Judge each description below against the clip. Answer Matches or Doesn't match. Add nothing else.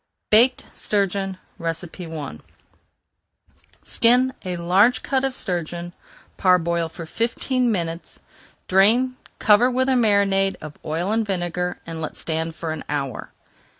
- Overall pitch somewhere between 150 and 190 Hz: Matches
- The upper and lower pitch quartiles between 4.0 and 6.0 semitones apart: Matches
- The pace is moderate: Doesn't match